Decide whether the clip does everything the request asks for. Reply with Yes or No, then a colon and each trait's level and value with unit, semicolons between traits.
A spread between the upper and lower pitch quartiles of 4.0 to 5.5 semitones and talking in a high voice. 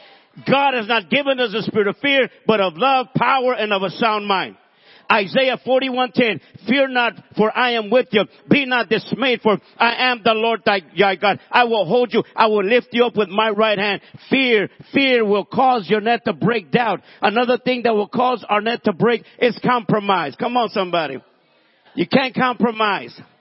No: average, 3.2 semitones; high, 225 Hz